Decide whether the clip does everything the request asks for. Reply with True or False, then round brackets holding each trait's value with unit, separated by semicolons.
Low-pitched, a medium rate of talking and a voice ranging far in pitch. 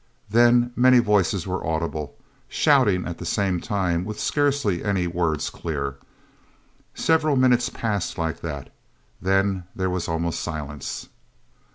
False (95 Hz; 130 wpm; 6.1 semitones)